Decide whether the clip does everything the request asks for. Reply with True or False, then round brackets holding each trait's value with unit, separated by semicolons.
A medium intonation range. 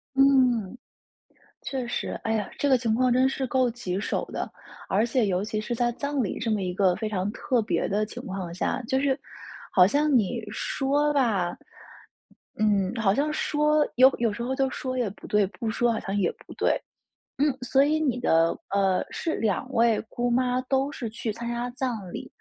True (4.1 semitones)